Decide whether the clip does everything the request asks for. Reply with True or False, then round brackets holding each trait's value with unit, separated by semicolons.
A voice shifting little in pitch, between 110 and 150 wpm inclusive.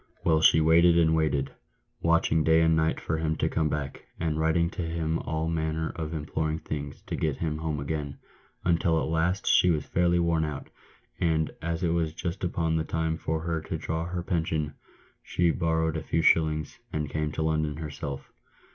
False (1.1 semitones; 190 wpm)